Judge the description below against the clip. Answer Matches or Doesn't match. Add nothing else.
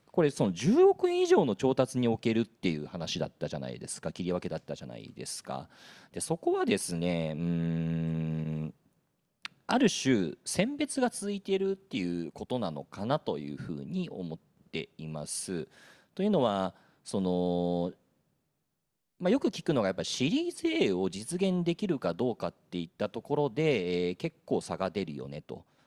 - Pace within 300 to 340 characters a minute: Matches